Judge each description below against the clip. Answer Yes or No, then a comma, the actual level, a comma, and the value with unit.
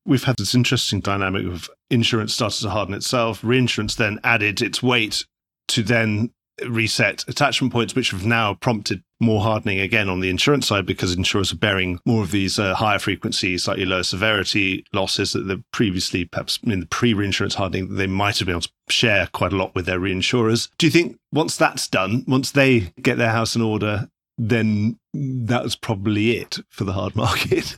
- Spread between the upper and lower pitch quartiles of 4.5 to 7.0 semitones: No, average, 3.5 semitones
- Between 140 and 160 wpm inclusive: No, average, 190 wpm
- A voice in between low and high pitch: No, low, 110 Hz